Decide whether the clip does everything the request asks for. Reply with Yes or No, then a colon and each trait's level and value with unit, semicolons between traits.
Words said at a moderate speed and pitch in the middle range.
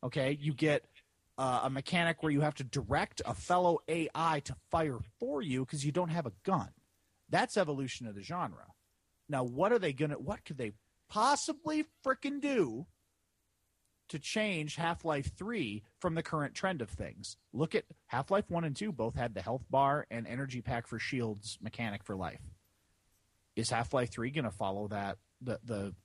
No: average, 185 wpm; low, 130 Hz